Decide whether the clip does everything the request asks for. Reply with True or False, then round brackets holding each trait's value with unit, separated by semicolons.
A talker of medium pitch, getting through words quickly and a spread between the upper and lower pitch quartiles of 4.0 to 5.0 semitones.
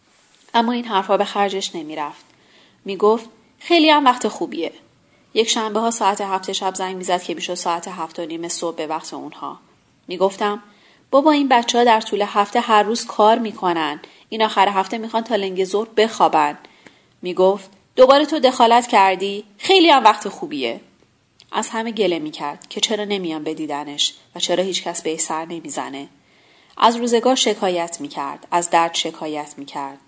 False (195 Hz; 180 wpm; 4.7 semitones)